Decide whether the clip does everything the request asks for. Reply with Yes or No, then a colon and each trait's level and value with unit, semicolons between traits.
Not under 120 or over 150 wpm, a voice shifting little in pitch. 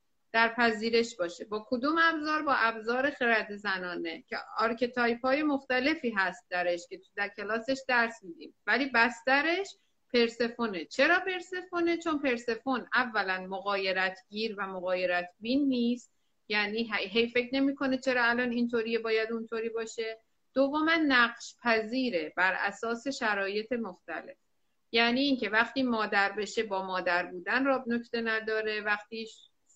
No: average, 135 wpm; average, 3.7 semitones